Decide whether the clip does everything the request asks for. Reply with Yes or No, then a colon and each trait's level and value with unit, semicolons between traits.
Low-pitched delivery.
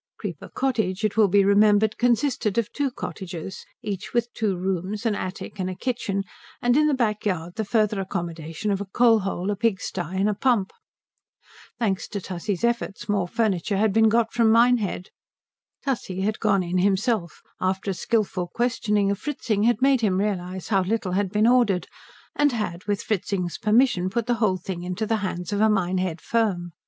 No: high, 205 Hz